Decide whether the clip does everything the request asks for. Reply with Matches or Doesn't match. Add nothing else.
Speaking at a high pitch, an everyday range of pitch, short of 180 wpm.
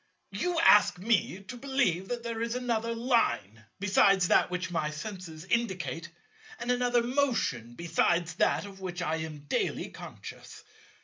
Doesn't match